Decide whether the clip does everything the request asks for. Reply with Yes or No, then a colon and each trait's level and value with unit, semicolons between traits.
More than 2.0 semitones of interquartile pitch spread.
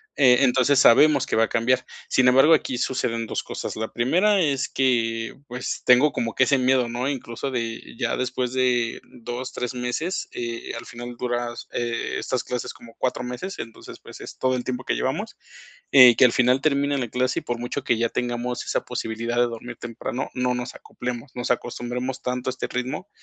No: narrow, 1.4 semitones